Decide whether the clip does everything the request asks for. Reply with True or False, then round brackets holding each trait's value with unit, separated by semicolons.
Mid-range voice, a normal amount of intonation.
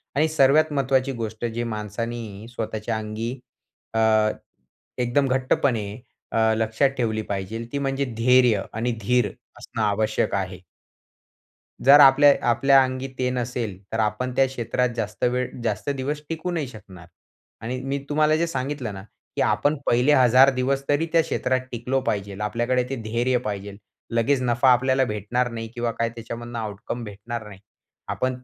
False (120 Hz; 3.4 semitones)